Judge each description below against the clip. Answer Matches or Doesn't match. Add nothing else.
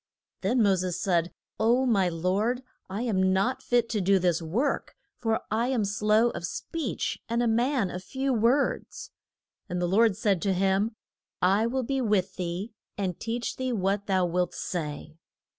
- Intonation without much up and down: Doesn't match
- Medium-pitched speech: Doesn't match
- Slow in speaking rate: Doesn't match